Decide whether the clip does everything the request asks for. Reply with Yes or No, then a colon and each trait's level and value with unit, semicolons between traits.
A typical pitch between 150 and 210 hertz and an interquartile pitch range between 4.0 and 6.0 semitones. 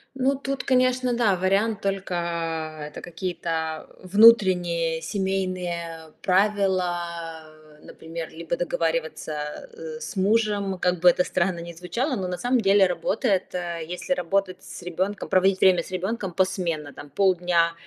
No: medium, 185 Hz; average, 3.3 semitones